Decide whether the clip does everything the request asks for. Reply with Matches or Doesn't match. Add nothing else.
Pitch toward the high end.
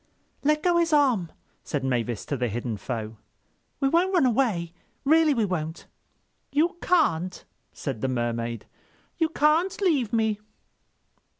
Matches